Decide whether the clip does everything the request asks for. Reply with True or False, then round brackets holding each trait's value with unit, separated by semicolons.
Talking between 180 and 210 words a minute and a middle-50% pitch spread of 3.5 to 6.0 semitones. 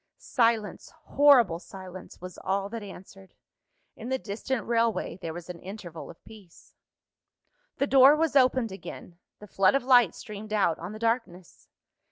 False (155 wpm; 4.7 semitones)